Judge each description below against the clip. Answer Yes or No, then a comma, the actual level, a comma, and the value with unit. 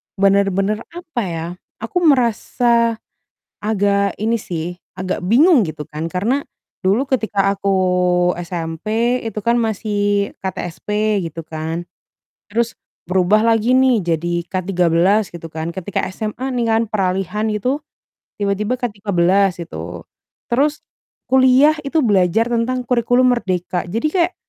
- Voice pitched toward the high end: Yes, high, 210 Hz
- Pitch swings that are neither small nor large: Yes, average, 4.6 semitones